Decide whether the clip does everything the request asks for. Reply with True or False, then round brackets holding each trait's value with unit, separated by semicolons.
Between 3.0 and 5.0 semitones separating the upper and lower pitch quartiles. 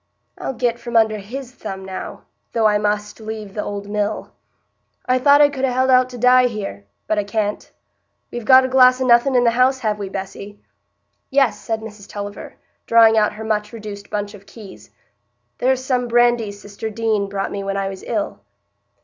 True (3.5 semitones)